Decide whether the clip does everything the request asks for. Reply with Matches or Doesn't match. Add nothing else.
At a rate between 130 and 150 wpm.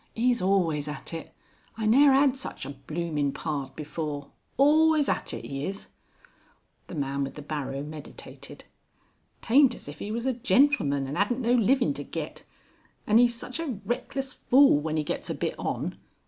Doesn't match